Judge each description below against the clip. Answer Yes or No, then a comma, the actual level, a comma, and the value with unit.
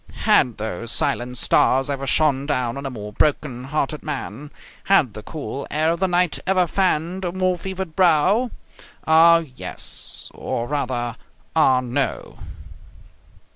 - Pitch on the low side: No, medium, 145 Hz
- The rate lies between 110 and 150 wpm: Yes, average, 140 wpm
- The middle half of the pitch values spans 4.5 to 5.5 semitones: Yes, average, 5.2 semitones